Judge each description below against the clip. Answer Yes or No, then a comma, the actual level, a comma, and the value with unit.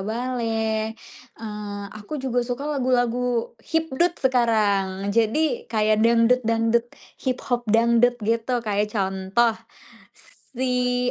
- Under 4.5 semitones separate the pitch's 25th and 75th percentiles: Yes, narrow, 2.4 semitones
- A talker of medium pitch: No, high, 230 Hz